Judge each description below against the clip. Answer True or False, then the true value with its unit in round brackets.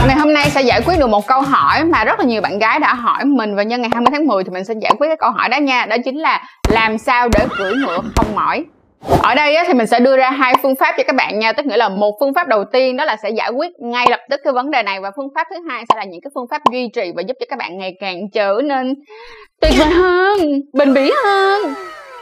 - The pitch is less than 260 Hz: False (270 Hz)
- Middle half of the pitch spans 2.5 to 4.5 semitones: False (5.1 semitones)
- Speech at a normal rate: False (290 wpm)